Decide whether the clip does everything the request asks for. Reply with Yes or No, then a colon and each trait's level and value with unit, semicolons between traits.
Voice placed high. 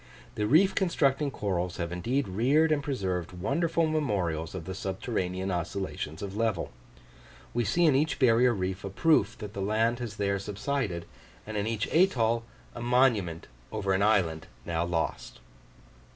No: low, 105 Hz